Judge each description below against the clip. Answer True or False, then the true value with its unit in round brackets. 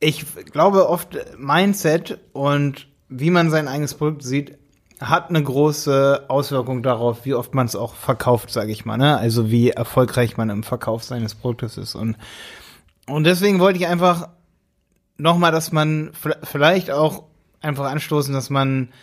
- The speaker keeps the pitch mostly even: False (4.2 semitones)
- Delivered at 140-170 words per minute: True (160 wpm)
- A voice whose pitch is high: False (140 Hz)